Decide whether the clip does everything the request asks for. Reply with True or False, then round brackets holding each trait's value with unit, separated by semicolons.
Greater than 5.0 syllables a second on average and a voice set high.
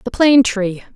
True (5.4 syllables/s; 230 Hz)